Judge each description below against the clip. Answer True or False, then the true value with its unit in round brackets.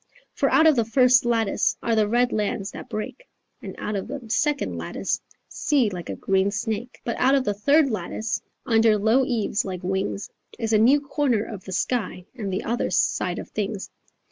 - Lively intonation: False (3.7 semitones)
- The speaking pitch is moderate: False (225 Hz)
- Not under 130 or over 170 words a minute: False (195 wpm)